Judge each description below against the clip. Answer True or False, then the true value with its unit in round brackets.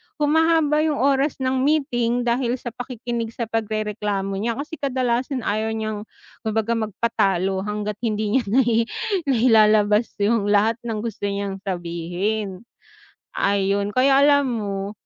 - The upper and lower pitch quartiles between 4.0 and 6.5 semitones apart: False (3.6 semitones)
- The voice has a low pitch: False (225 Hz)